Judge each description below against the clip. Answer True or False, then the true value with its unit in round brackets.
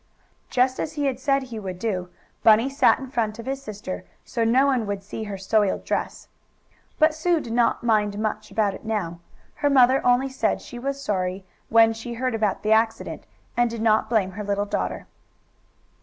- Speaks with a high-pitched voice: True (225 Hz)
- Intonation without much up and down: False (3.8 semitones)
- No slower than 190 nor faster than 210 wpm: True (195 wpm)